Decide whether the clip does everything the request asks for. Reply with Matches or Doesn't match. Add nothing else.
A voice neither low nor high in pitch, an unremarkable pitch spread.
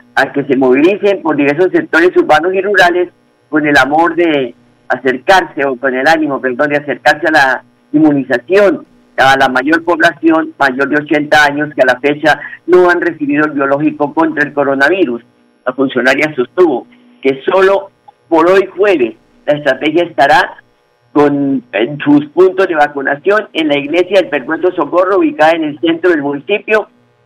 Matches